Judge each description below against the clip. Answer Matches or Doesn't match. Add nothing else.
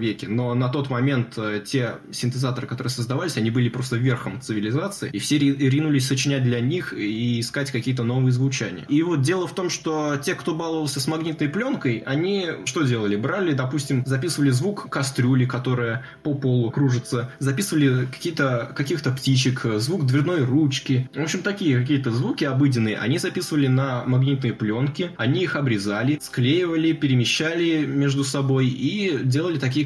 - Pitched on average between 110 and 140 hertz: Matches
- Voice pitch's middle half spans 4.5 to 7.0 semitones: Doesn't match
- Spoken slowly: Doesn't match